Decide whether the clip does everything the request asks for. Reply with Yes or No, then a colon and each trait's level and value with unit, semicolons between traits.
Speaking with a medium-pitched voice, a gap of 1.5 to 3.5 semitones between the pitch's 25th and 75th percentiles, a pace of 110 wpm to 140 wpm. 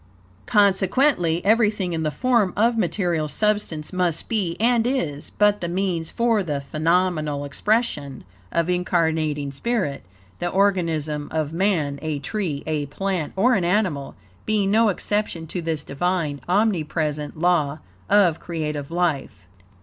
No: medium, 175 Hz; average, 5.0 semitones; slow, 135 wpm